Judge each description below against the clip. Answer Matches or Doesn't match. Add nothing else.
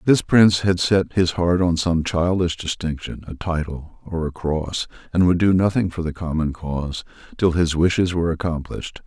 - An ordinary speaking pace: Matches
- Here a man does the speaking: Matches